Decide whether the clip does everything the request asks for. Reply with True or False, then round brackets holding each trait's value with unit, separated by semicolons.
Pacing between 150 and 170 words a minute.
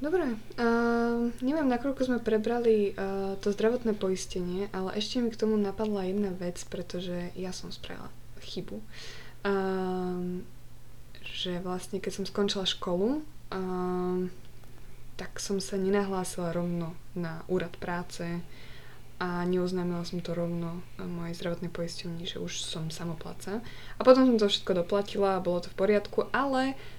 False (140 wpm)